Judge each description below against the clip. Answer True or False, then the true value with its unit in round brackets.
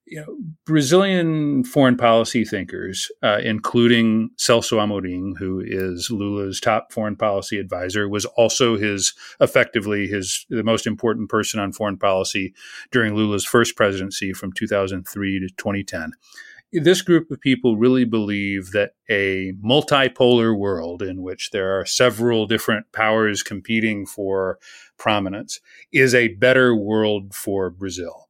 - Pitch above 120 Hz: False (110 Hz)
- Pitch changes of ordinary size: True (3.8 semitones)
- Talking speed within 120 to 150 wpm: True (135 wpm)